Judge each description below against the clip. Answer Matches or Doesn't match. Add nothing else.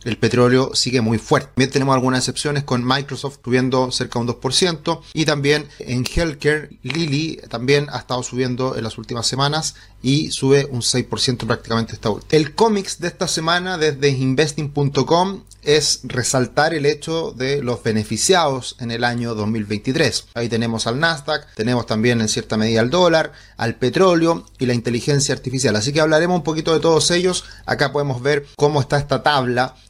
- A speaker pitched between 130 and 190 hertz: Matches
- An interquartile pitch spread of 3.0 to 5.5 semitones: Matches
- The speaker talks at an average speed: Matches